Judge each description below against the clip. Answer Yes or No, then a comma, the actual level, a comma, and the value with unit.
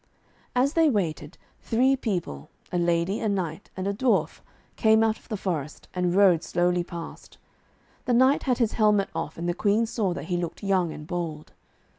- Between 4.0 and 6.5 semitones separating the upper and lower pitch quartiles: Yes, average, 4.4 semitones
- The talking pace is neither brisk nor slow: Yes, average, 185 wpm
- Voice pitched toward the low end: No, high, 190 Hz